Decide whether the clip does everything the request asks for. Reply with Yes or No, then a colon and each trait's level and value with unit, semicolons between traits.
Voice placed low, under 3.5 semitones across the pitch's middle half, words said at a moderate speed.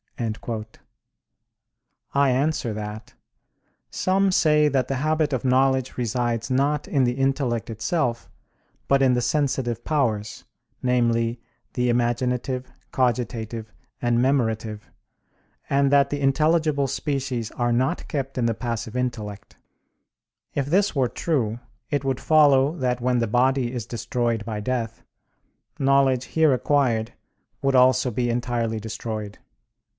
No: low, 125 Hz; average, 2.9 semitones; slow, 125 wpm